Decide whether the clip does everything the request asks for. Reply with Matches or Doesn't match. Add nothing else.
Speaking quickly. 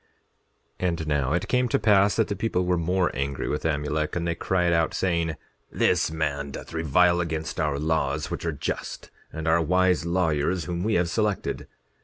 Doesn't match